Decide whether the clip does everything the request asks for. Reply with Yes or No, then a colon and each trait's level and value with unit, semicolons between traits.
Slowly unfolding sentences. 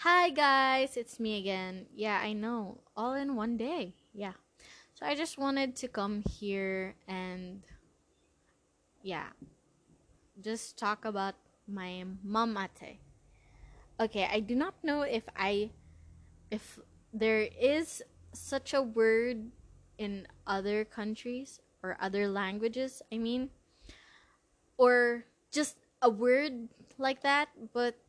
Yes: slow, 120 wpm